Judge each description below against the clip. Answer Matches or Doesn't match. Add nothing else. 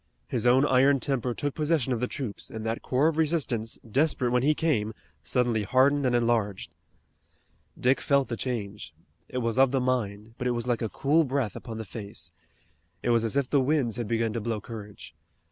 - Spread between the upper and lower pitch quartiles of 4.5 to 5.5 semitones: Doesn't match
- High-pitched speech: Doesn't match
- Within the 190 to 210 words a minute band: Matches